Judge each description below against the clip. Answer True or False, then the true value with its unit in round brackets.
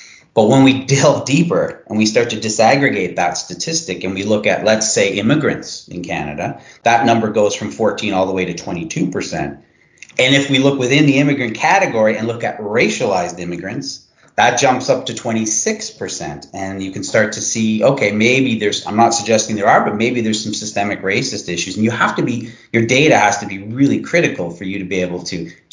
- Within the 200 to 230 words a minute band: True (205 wpm)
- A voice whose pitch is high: False (110 Hz)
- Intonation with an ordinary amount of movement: True (3.2 semitones)